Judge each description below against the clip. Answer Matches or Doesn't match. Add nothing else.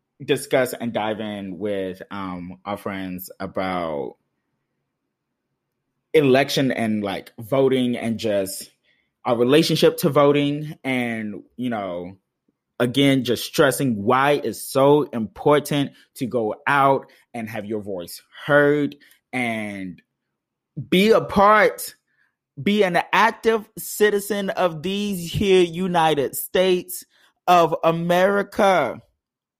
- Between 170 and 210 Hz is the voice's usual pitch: Doesn't match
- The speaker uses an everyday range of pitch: Doesn't match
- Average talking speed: Doesn't match